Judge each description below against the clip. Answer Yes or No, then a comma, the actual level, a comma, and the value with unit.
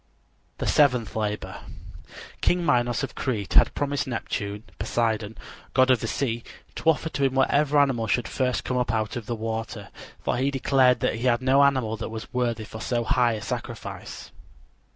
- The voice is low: Yes, low, 120 Hz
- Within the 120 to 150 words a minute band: No, average, 175 wpm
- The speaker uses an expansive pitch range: No, average, 3.1 semitones